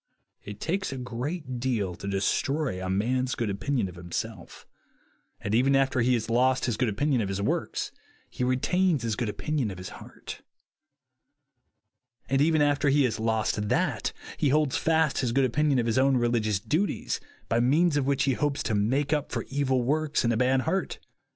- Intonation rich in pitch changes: No, average, 4.4 semitones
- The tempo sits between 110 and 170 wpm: No, average, 190 wpm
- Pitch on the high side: No, low, 130 Hz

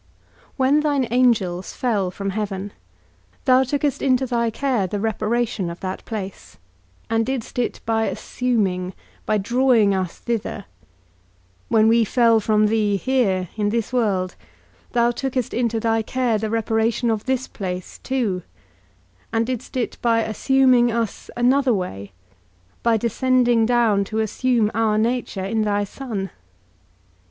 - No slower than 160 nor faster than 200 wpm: No, average, 140 wpm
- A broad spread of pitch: No, average, 3.2 semitones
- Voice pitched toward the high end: Yes, high, 225 Hz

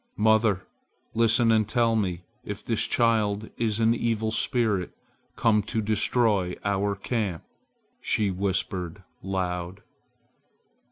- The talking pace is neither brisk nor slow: No, slow, 110 wpm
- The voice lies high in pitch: No, low, 105 Hz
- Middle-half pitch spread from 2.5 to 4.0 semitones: Yes, average, 2.8 semitones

